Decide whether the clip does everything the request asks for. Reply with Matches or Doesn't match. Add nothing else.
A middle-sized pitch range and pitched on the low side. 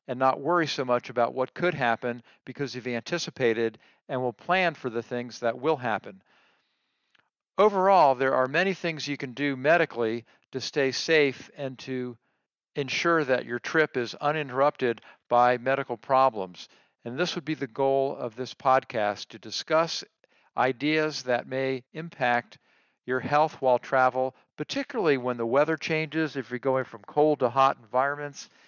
Matches